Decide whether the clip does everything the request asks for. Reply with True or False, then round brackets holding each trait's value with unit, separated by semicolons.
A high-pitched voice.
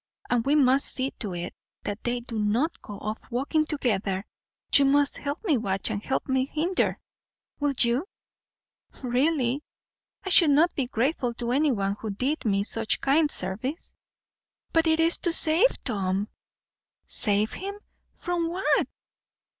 True (260 Hz)